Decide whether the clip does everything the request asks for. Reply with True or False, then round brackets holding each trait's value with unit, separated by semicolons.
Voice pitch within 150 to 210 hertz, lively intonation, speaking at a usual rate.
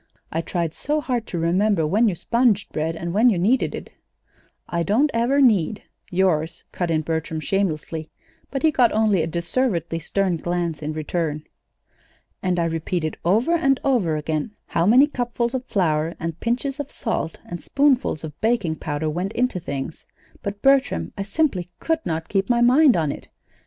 True (185 Hz; 6.7 semitones; 175 wpm)